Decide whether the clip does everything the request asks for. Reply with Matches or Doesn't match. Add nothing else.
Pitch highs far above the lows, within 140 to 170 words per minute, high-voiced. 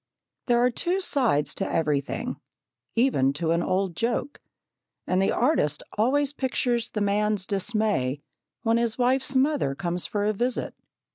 Matches